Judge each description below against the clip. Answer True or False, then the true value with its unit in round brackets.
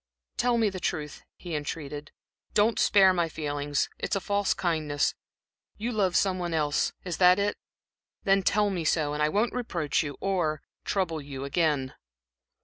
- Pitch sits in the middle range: True (170 Hz)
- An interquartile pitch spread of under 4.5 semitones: False (4.8 semitones)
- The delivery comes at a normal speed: True (160 wpm)